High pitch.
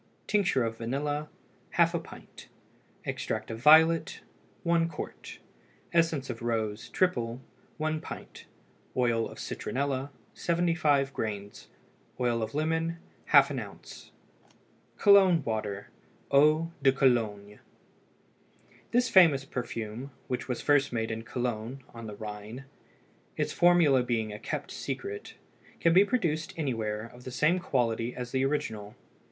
No: low, 130 Hz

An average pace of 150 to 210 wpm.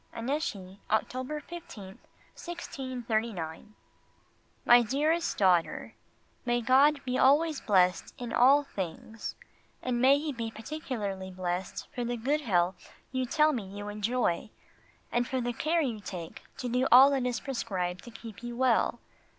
No: average, 140 wpm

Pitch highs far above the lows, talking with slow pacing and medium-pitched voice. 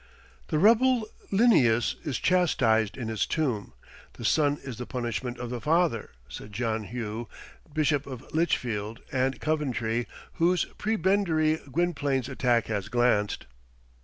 No: wide, 5.7 semitones; slow, 130 wpm; low, 130 Hz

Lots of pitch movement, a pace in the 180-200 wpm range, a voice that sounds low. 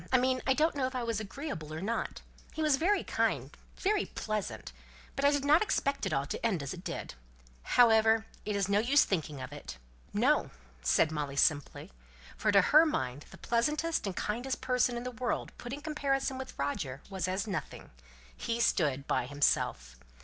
No: wide, 8.9 semitones; average, 195 wpm; high, 230 Hz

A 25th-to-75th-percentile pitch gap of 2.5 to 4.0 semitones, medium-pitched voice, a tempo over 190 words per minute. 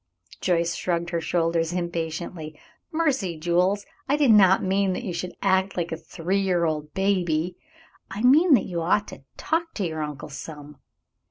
No: average, 3.2 semitones; medium, 175 Hz; average, 175 wpm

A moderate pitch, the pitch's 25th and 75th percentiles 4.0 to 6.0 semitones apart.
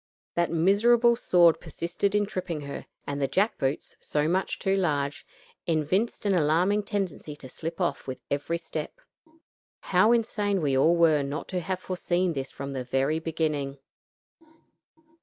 Yes: medium, 170 Hz; average, 4.8 semitones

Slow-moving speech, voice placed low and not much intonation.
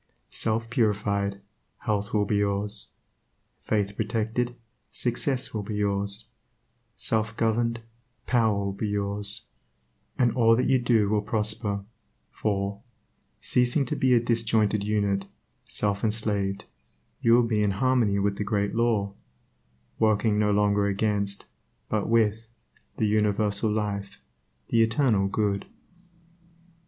Yes: slow, 125 wpm; low, 105 Hz; narrow, 2.1 semitones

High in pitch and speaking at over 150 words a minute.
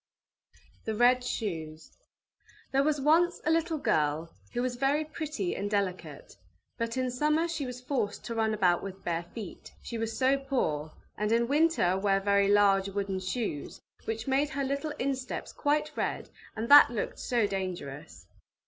Yes: high, 230 Hz; average, 165 wpm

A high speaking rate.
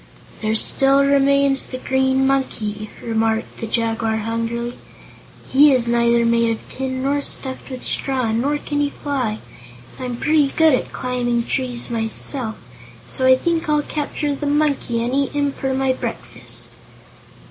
No: average, 150 wpm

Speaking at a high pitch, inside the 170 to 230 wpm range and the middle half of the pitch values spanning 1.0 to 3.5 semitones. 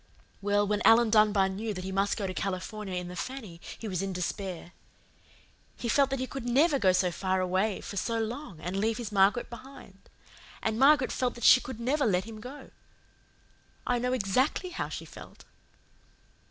No: high, 215 Hz; average, 190 wpm; average, 4.6 semitones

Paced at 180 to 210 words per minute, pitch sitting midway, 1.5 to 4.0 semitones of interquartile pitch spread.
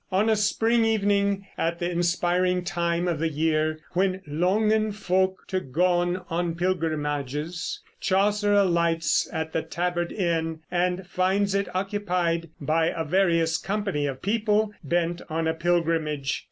No: average, 140 wpm; medium, 175 Hz; average, 3.1 semitones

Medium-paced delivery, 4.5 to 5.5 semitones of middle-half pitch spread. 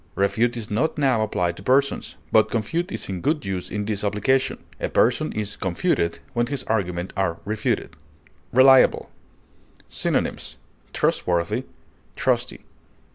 No: slow, 130 wpm; average, 5.2 semitones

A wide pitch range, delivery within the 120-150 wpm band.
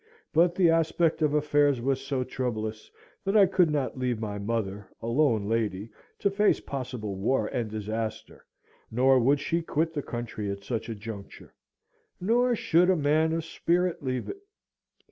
No: wide, 6.6 semitones; average, 165 wpm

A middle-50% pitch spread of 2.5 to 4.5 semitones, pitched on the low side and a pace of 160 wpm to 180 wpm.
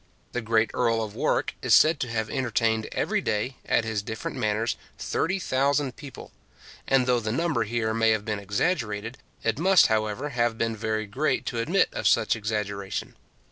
Yes: average, 3.1 semitones; low, 115 Hz; average, 175 wpm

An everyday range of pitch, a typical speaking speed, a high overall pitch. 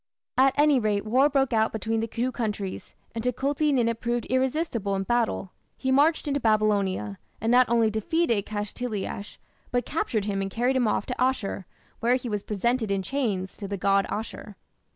Yes: average, 3.9 semitones; average, 180 wpm; high, 230 Hz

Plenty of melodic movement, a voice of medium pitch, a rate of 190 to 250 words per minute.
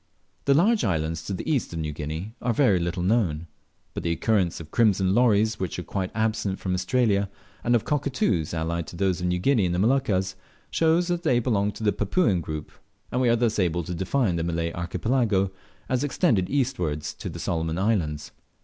No: wide, 5.9 semitones; low, 100 Hz; average, 200 wpm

